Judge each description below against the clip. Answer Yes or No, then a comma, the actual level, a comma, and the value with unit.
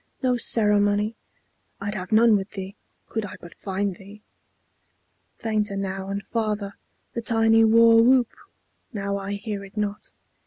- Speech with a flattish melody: Yes, narrow, 2.1 semitones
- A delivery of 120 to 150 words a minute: Yes, average, 145 wpm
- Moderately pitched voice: No, high, 210 Hz